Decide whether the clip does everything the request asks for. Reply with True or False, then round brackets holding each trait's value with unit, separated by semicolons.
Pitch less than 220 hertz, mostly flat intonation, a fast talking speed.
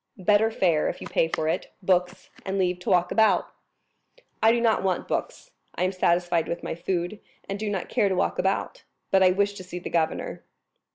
True (185 Hz; 2.3 semitones; 210 wpm)